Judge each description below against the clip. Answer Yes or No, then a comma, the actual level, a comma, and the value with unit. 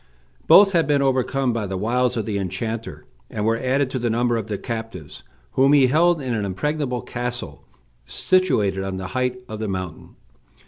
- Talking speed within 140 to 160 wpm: No, average, 185 wpm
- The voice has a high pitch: No, low, 120 Hz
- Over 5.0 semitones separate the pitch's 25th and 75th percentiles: No, average, 4.4 semitones